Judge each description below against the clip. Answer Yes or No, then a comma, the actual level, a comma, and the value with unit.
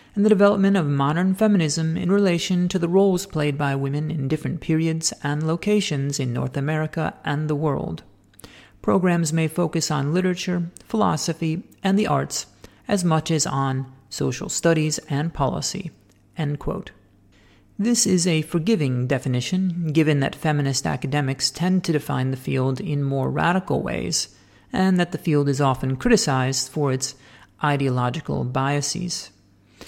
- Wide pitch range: No, average, 4.6 semitones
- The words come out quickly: No, average, 145 wpm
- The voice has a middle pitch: Yes, medium, 150 Hz